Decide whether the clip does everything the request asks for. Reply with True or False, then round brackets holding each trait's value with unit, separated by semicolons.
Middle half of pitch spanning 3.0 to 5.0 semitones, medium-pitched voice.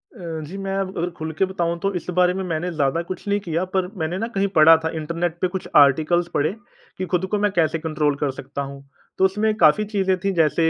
True (3.4 semitones; 175 Hz)